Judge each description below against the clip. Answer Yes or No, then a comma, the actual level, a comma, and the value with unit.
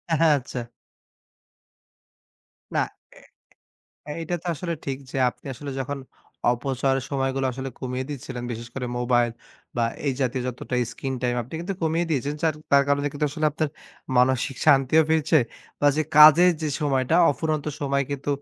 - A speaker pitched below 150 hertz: Yes, medium, 140 Hz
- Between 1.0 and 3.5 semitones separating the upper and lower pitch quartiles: Yes, average, 2.9 semitones